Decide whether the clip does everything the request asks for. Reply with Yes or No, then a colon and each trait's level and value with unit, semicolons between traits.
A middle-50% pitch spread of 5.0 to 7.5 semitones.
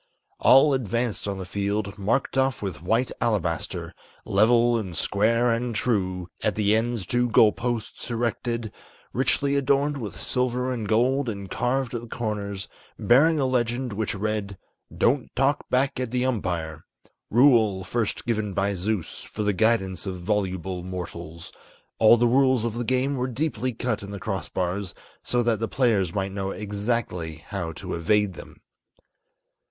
No: average, 3.9 semitones